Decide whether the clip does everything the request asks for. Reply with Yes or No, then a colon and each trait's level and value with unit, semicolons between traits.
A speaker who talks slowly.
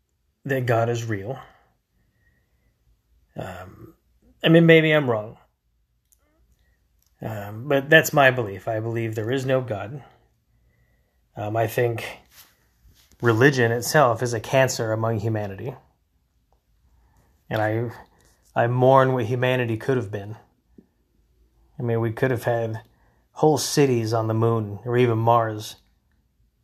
Yes: slow, 125 wpm